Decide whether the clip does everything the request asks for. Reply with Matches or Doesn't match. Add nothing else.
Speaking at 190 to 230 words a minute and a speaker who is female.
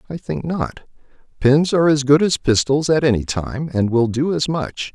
Doesn't match